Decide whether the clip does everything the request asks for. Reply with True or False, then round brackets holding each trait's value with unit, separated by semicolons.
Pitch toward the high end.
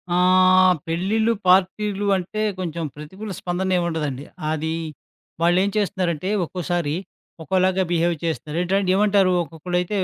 False (180 Hz)